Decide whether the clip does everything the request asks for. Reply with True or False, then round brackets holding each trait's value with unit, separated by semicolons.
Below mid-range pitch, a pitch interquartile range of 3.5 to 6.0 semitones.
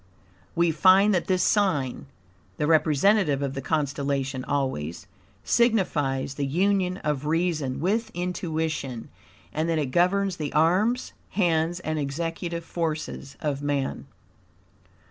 False (160 Hz; 4.3 semitones)